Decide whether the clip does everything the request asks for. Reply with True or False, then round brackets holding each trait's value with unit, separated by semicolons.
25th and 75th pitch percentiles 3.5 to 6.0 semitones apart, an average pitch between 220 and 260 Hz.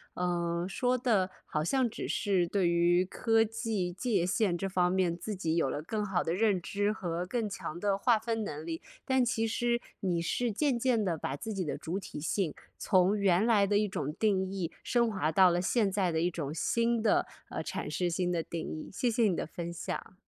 False (4.3 semitones; 190 Hz)